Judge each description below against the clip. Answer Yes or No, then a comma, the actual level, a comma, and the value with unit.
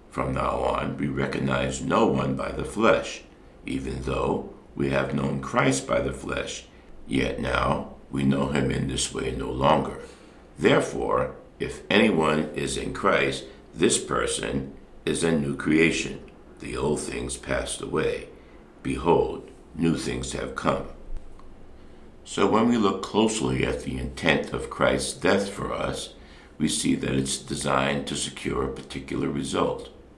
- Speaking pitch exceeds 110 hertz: No, very low, 70 Hz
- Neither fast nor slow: Yes, average, 145 wpm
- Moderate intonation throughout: No, narrow, 1.2 semitones